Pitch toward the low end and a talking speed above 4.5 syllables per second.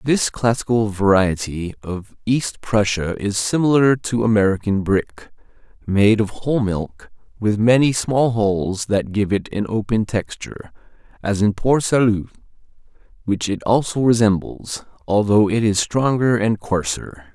No: low, 105 Hz; 4.3 syllables/s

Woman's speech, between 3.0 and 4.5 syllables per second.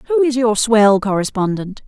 Yes: female; 4.4 syllables/s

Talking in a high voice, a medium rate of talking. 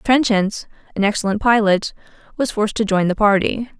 Yes: high, 210 Hz; average, 160 wpm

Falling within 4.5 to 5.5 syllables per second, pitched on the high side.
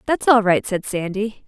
Yes: 4.6 syllables/s; high, 210 Hz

